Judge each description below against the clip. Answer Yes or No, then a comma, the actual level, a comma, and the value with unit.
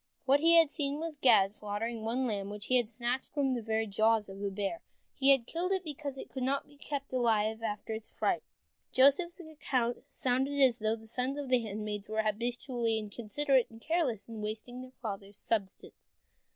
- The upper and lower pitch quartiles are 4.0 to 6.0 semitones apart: Yes, average, 4.3 semitones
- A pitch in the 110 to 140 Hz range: No, high, 240 Hz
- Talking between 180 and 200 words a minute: Yes, average, 195 wpm